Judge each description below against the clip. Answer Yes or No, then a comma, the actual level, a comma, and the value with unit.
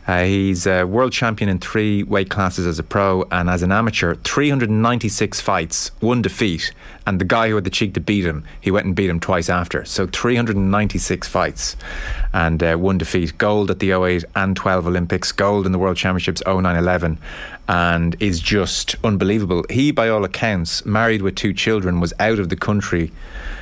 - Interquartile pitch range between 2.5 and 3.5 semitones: Yes, average, 2.9 semitones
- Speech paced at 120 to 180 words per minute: No, average, 190 wpm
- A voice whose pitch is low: Yes, very low, 95 Hz